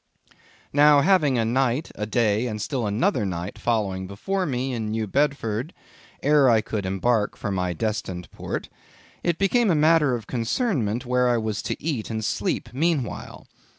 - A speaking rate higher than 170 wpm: No, average, 165 wpm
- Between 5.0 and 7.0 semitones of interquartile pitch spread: Yes, wide, 5.5 semitones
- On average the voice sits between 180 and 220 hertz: No, low, 120 Hz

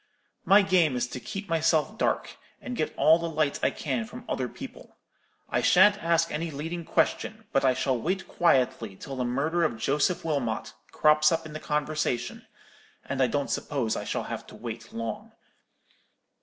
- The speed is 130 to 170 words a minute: No, average, 180 wpm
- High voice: No, medium, 150 Hz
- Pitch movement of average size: Yes, average, 4.5 semitones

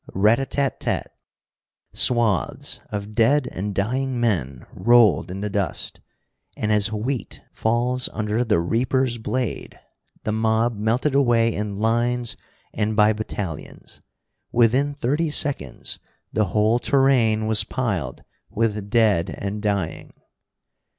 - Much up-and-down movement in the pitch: No, average, 2.9 semitones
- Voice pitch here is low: Yes, low, 110 Hz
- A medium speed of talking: No, slow, 125 wpm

